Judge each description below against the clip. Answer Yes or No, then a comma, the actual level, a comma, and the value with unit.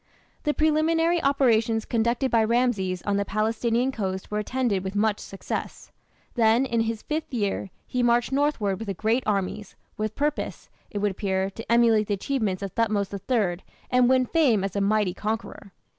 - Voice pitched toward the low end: No, high, 220 Hz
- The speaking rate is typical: Yes, average, 175 wpm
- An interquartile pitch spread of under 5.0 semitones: Yes, average, 3.8 semitones